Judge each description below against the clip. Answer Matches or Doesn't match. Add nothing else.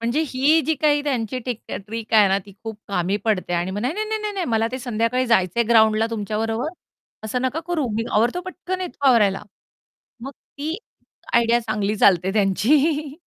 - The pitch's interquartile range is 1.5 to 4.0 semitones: Doesn't match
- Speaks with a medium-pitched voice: Doesn't match